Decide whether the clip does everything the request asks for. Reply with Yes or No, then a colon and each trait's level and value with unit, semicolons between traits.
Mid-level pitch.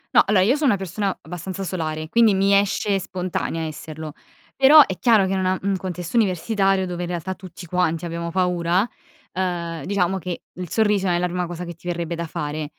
Yes: medium, 180 Hz